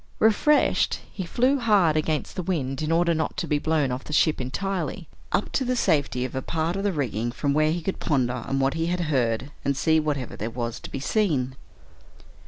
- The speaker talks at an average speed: No, fast, 215 wpm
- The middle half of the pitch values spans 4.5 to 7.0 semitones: Yes, average, 4.9 semitones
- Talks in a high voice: No, medium, 155 Hz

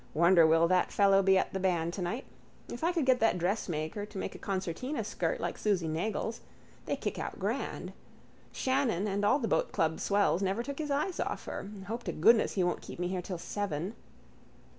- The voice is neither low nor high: No, high, 195 Hz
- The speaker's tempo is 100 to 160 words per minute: No, average, 200 wpm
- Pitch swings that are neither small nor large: Yes, average, 4.5 semitones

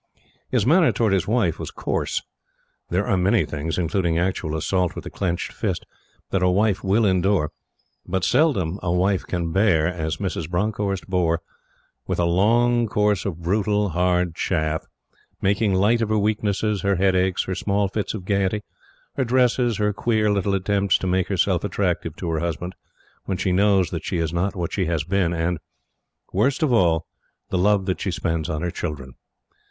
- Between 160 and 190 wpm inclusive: Yes, average, 180 wpm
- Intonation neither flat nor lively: Yes, average, 3.1 semitones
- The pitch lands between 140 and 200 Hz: No, very low, 95 Hz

